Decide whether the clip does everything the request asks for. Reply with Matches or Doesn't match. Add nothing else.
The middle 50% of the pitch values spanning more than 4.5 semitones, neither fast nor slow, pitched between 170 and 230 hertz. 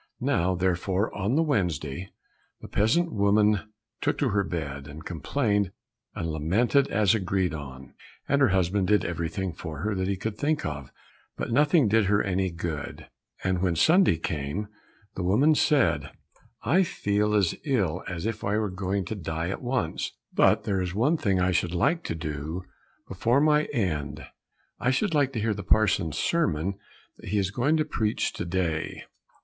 Doesn't match